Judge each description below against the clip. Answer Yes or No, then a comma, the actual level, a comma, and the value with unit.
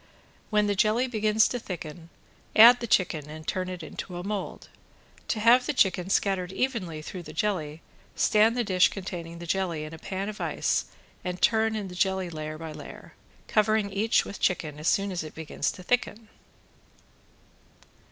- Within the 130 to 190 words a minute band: Yes, average, 180 wpm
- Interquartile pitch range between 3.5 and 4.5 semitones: Yes, average, 4.1 semitones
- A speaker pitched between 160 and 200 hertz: Yes, high, 190 Hz